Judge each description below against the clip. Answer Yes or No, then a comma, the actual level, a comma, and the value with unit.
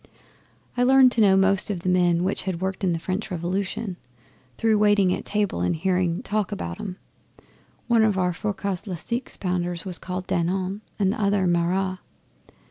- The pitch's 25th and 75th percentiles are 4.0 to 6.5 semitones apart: No, narrow, 2.5 semitones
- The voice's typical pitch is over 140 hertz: Yes, high, 190 Hz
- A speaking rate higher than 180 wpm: No, average, 165 wpm